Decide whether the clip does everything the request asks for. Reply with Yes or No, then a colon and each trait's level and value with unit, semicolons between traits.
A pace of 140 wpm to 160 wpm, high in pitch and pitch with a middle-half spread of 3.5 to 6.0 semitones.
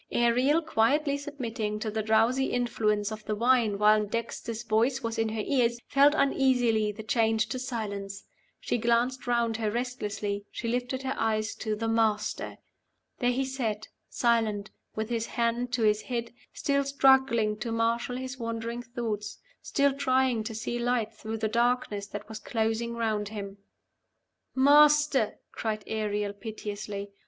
No: average, 150 wpm; high, 230 Hz; narrow, 2.6 semitones